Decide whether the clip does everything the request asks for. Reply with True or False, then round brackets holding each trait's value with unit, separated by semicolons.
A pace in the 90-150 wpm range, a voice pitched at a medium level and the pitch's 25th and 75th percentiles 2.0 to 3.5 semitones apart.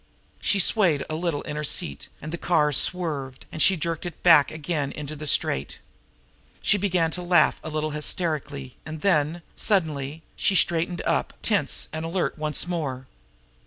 False (165 wpm; 155 Hz; 2.8 semitones)